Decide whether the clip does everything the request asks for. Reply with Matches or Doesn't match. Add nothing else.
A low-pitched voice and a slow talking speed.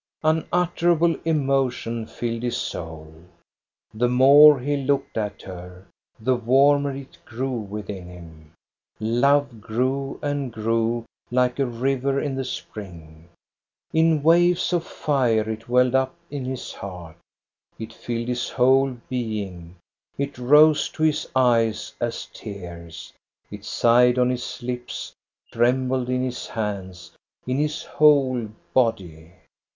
Matches